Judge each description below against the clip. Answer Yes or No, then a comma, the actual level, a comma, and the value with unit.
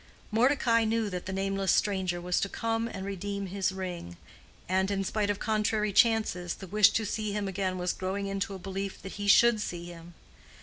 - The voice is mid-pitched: No, high, 195 Hz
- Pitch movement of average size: No, narrow, 2.2 semitones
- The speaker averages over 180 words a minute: Yes, average, 200 wpm